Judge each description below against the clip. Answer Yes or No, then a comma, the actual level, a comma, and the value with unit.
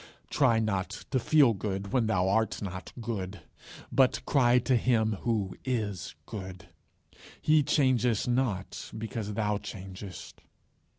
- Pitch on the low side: Yes, low, 110 Hz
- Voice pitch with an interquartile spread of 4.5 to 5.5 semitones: No, average, 4.1 semitones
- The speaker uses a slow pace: Yes, slow, 125 wpm